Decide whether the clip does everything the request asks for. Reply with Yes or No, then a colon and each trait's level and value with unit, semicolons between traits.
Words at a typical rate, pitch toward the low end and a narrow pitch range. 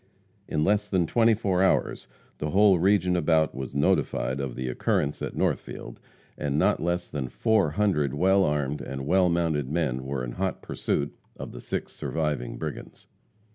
No: average, 170 wpm; very low, 80 Hz; average, 5.2 semitones